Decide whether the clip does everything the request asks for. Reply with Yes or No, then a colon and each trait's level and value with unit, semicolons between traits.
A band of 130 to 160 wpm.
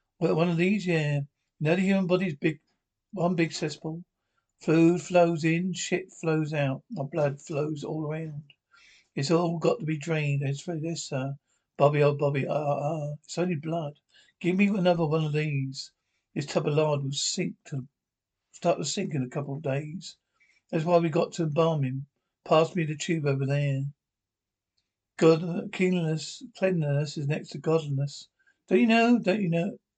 No: average, 190 wpm